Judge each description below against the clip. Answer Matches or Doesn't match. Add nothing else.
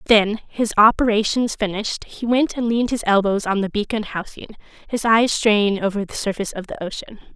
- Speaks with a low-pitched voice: Doesn't match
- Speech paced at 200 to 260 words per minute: Doesn't match